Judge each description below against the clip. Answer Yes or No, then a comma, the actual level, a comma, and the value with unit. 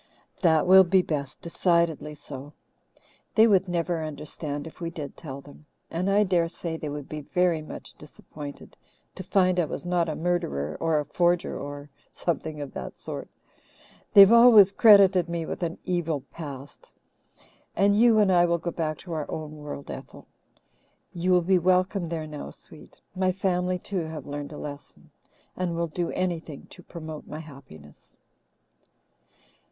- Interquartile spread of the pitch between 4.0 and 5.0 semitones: No, average, 3.3 semitones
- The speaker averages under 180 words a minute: Yes, average, 165 wpm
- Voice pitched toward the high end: No, medium, 170 Hz